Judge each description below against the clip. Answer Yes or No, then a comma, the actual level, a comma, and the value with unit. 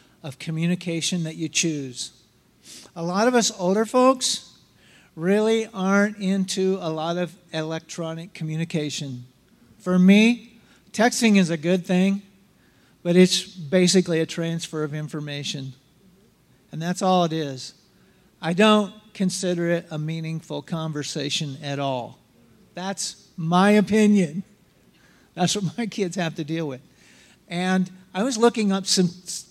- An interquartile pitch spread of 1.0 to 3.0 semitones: No, average, 3.4 semitones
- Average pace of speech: No, slow, 130 wpm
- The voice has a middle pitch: Yes, medium, 180 Hz